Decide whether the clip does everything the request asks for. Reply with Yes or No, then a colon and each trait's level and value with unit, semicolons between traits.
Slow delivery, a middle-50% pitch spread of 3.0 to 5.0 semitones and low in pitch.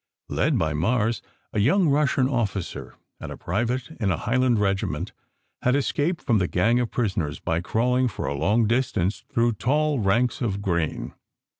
No: average, 165 wpm; average, 4.6 semitones; low, 115 Hz